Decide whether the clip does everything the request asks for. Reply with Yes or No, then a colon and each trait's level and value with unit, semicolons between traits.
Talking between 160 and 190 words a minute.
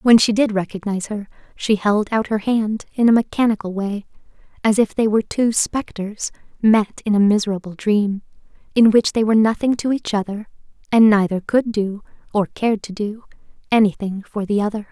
Yes: average, 180 wpm